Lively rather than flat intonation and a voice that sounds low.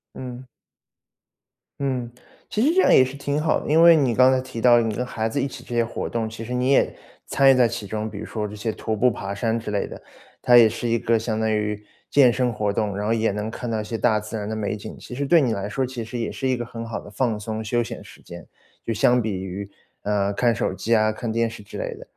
No: average, 2.8 semitones; low, 115 Hz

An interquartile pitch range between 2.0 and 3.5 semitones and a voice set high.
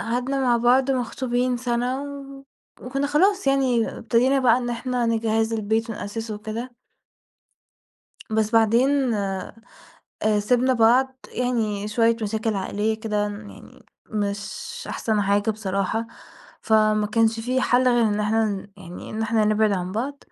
Yes: average, 2.9 semitones; high, 225 Hz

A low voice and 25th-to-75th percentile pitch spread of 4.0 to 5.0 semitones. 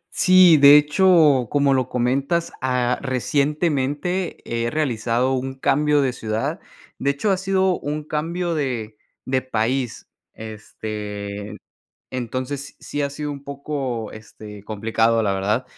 Yes: low, 130 Hz; average, 4.5 semitones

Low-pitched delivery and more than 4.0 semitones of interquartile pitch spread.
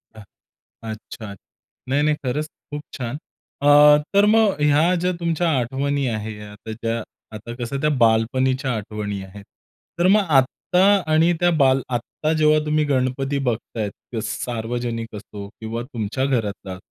Yes: low, 125 Hz; average, 5.1 semitones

